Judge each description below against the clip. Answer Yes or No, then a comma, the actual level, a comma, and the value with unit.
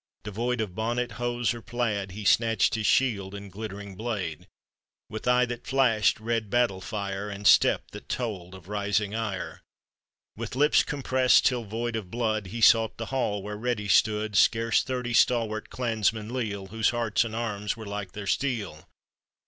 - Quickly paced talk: No, average, 170 wpm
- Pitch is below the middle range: Yes, low, 110 Hz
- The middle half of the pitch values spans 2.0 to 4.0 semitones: Yes, average, 2.8 semitones